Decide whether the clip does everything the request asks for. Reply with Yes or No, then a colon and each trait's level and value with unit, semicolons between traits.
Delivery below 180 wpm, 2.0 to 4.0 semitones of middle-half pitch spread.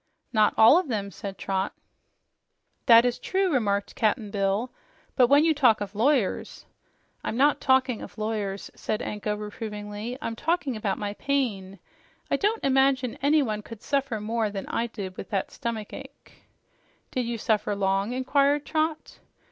No: average, 160 wpm; average, 4.6 semitones